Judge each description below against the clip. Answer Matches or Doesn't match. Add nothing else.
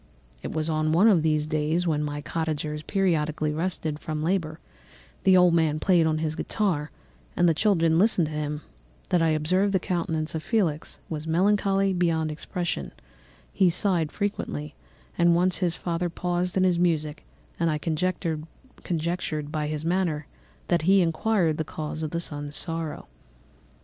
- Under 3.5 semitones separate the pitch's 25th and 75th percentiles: Matches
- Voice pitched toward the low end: Doesn't match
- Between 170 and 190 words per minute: Doesn't match